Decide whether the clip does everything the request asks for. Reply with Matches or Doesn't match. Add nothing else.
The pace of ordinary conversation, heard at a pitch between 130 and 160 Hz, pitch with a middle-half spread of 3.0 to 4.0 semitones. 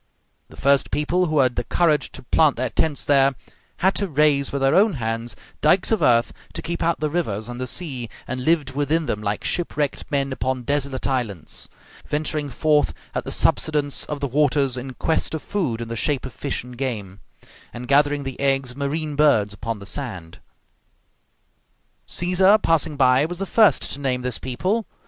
Matches